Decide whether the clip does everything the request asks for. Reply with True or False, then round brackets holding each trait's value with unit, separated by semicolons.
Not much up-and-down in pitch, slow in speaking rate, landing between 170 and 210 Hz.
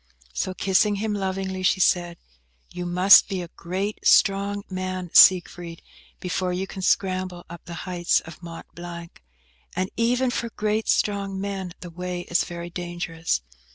False (2.1 semitones; 155 wpm; 185 Hz)